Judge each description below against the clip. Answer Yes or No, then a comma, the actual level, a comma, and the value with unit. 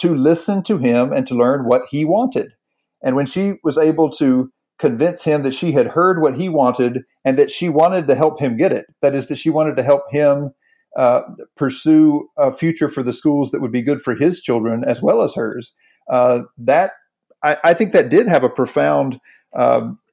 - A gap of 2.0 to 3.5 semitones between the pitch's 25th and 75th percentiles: No, average, 4.4 semitones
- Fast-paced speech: Yes, fast, 210 wpm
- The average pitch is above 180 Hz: No, medium, 150 Hz